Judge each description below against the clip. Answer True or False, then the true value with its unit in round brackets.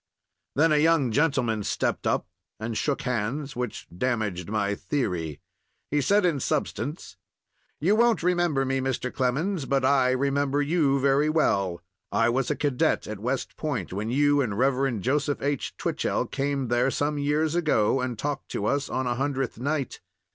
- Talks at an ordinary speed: True (165 wpm)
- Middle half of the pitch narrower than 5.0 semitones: True (3.4 semitones)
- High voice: False (135 Hz)